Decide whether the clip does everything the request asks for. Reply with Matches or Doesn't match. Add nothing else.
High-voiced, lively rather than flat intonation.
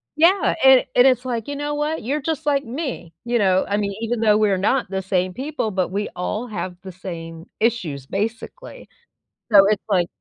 Matches